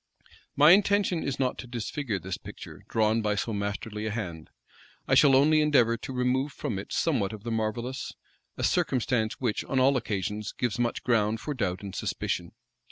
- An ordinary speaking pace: Yes, average, 180 wpm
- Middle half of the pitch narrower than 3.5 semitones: No, average, 4.1 semitones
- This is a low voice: Yes, low, 115 Hz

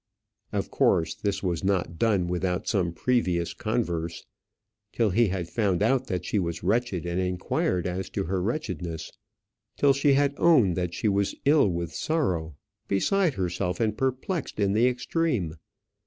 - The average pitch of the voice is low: Yes, low, 100 Hz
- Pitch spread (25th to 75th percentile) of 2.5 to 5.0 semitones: No, wide, 5.5 semitones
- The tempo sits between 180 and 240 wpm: No, average, 155 wpm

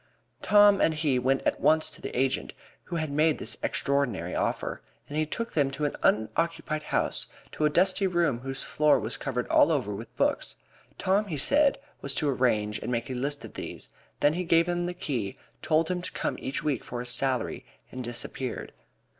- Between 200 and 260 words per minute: Yes, fast, 205 wpm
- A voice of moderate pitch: Yes, medium, 145 Hz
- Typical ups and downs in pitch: Yes, average, 4.8 semitones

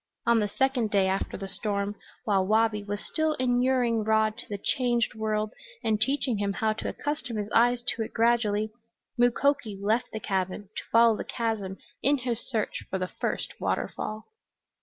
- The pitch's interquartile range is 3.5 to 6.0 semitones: No, average, 2.8 semitones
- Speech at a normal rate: Yes, average, 175 wpm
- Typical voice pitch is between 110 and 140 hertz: No, high, 220 Hz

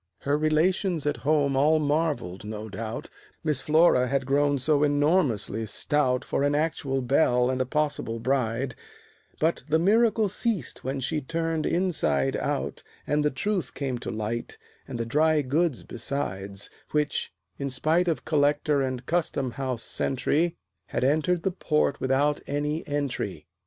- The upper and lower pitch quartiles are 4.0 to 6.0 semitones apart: No, average, 3.6 semitones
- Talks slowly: No, average, 150 wpm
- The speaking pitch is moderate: Yes, medium, 145 Hz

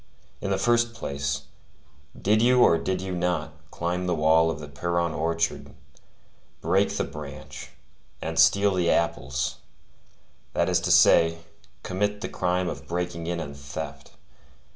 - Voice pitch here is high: No, very low, 85 Hz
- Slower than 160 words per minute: Yes, average, 145 wpm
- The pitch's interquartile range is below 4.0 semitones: Yes, average, 2.7 semitones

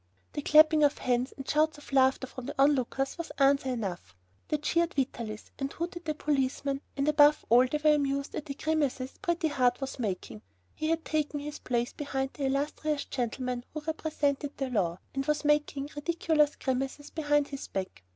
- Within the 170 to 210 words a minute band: Yes, average, 180 wpm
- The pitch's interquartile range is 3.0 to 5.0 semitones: No, narrow, 2.6 semitones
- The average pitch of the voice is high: Yes, very high, 280 Hz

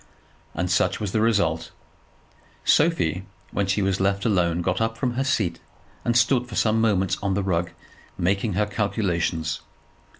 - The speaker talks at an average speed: Yes, average, 160 wpm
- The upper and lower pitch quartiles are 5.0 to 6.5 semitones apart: No, average, 4.0 semitones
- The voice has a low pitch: Yes, low, 100 Hz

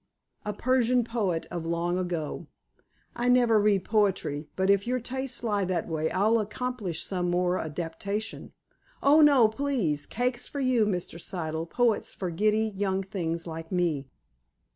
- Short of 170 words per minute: Yes, average, 150 wpm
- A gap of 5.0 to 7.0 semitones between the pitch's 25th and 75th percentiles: Yes, wide, 5.6 semitones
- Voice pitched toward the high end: Yes, high, 200 Hz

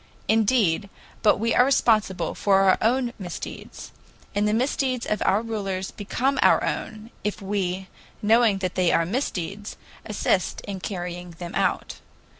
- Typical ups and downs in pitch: Yes, average, 3.3 semitones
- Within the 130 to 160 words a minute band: Yes, average, 145 wpm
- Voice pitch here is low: No, high, 205 Hz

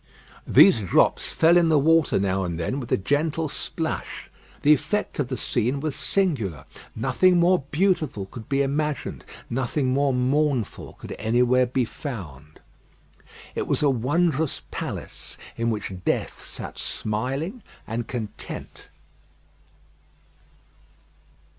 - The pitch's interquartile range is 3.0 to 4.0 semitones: No, average, 5.3 semitones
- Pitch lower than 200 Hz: Yes, low, 135 Hz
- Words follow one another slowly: Yes, slow, 125 wpm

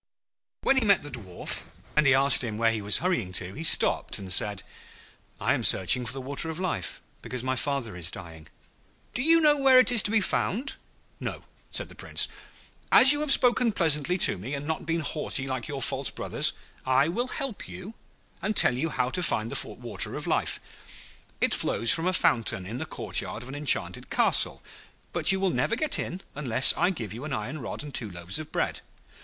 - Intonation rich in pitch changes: Yes, wide, 8.5 semitones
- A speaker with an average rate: No, fast, 210 wpm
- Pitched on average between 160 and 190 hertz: No, medium, 140 Hz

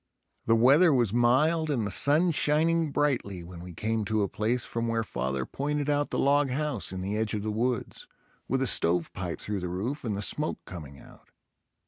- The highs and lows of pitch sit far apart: Yes, wide, 6.6 semitones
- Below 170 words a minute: No, average, 200 wpm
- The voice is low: Yes, low, 115 Hz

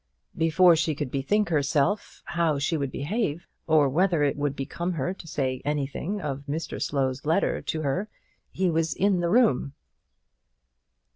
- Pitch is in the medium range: Yes, medium, 155 Hz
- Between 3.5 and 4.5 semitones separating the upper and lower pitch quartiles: Yes, average, 4.0 semitones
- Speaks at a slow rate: No, average, 160 wpm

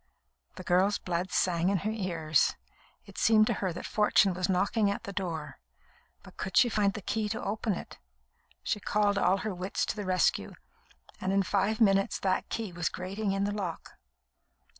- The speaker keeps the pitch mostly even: Yes, narrow, 2.2 semitones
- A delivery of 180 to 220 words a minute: Yes, average, 185 wpm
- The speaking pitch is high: Yes, high, 195 Hz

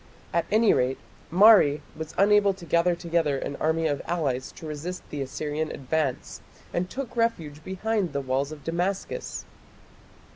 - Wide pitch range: No, average, 4.5 semitones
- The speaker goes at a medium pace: Yes, average, 150 wpm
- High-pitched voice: No, medium, 165 Hz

